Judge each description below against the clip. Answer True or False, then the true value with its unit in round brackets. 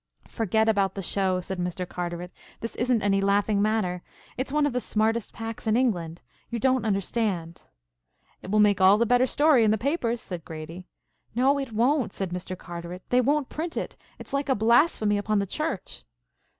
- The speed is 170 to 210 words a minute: True (190 wpm)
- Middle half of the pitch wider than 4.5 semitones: True (4.9 semitones)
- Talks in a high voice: True (215 Hz)